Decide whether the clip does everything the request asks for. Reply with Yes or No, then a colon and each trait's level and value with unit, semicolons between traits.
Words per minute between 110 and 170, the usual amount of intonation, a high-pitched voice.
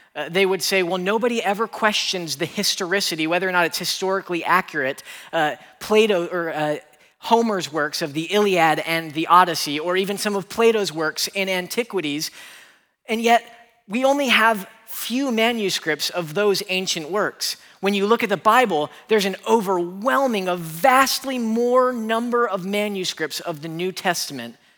Yes: average, 160 wpm; average, 4.7 semitones; high, 195 Hz